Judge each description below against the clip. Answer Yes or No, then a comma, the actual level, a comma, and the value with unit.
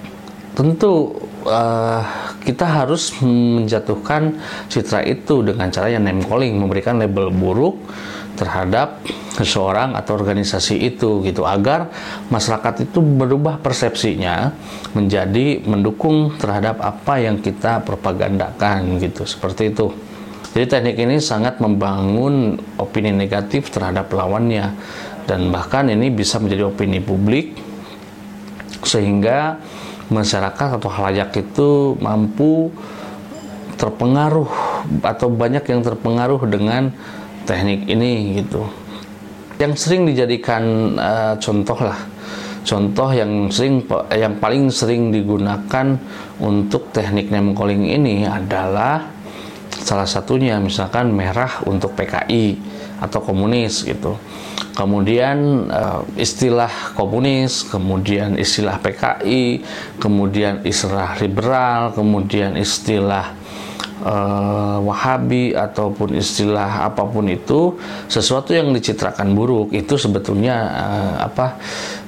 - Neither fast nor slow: Yes, average, 100 wpm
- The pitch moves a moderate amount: Yes, average, 3.2 semitones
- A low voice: Yes, low, 105 Hz